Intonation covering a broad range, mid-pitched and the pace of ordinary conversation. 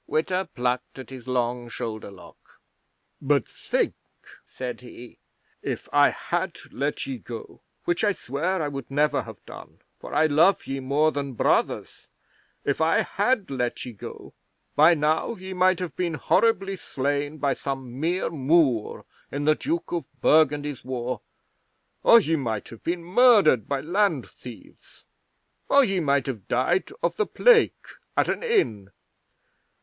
Yes: wide, 5.8 semitones; medium, 145 Hz; average, 155 wpm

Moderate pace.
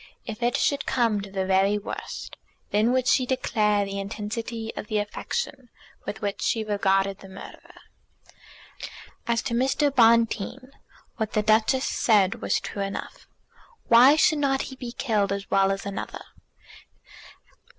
Yes: average, 150 wpm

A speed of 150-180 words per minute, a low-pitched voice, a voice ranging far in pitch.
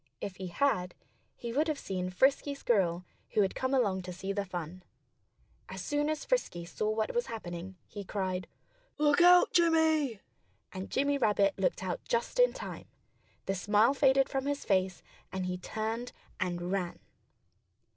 No: average, 165 wpm; high, 210 Hz; wide, 7.1 semitones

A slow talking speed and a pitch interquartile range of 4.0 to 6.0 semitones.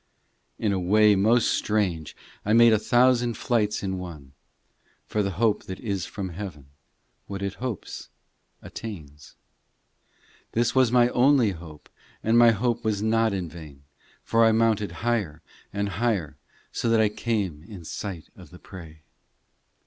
No: average, 155 wpm; average, 4.5 semitones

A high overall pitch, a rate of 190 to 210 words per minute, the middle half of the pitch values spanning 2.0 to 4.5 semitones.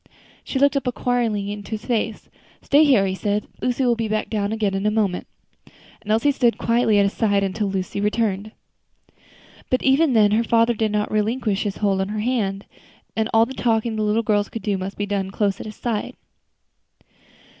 Yes: high, 215 Hz; average, 200 wpm; narrow, 2.4 semitones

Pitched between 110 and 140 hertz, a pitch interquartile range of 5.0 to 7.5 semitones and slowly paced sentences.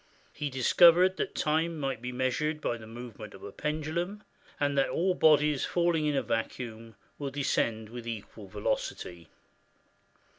No: low, 135 Hz; average, 5.3 semitones; average, 150 wpm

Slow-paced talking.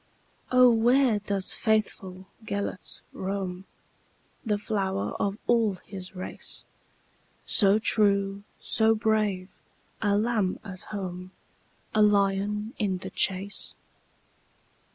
Yes: slow, 85 wpm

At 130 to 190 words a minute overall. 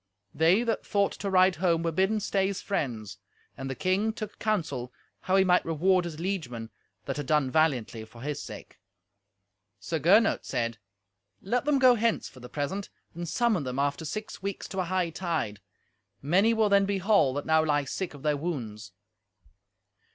Yes: average, 180 wpm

